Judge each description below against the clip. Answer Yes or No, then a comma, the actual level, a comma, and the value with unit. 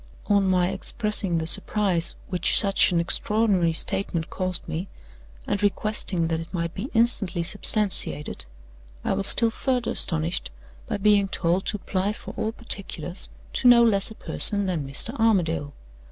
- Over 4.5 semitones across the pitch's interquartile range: No, average, 3.9 semitones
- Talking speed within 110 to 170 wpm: Yes, average, 155 wpm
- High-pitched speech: Yes, high, 195 Hz